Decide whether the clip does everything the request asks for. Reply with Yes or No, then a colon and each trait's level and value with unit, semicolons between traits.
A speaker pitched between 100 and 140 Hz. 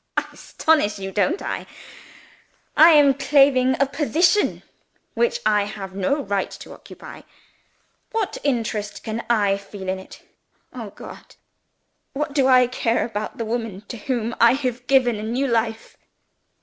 No: high, 240 Hz